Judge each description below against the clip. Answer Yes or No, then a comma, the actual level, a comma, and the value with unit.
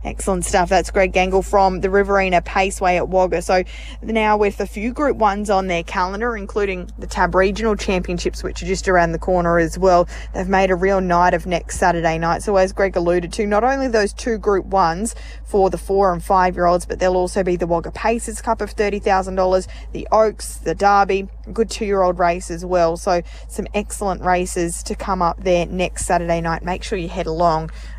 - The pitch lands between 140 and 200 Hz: Yes, medium, 185 Hz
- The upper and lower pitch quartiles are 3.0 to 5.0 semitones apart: No, narrow, 2.4 semitones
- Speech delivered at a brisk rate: Yes, fast, 215 wpm